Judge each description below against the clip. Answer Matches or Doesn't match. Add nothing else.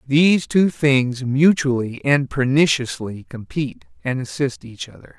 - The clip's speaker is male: Matches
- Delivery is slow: Matches